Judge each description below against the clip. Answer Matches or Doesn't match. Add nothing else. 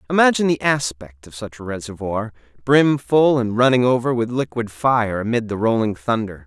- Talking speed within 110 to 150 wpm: Doesn't match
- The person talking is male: Matches